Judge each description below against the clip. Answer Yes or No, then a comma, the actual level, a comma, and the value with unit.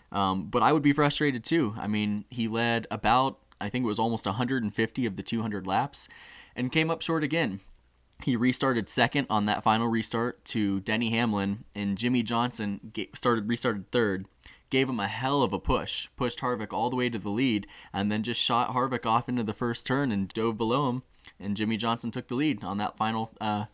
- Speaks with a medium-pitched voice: No, low, 115 Hz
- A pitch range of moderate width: Yes, average, 3.0 semitones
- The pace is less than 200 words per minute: No, fast, 205 wpm